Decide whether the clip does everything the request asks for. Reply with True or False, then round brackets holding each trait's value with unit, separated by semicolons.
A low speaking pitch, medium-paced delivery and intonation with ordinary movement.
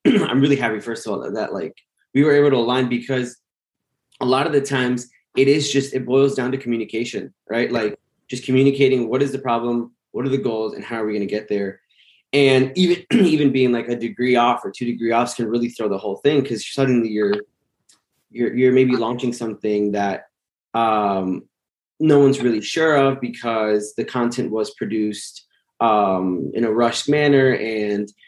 True (120 Hz; 195 wpm; 3.5 semitones)